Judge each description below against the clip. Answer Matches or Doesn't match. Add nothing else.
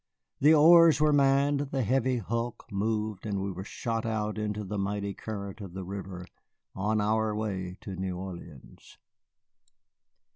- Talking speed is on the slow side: Doesn't match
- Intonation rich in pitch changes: Doesn't match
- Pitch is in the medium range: Doesn't match